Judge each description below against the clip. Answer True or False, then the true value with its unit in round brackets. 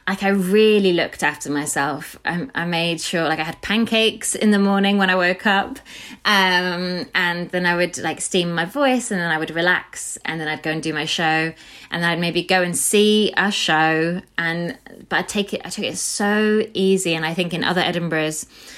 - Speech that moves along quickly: True (215 wpm)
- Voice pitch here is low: False (180 Hz)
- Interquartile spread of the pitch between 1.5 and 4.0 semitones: True (3.6 semitones)